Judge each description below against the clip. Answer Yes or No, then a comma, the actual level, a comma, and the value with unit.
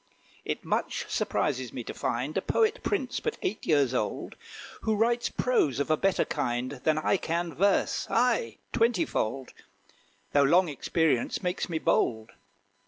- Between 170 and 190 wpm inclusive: No, average, 155 wpm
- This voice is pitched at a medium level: Yes, medium, 155 Hz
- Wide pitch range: Yes, wide, 7.4 semitones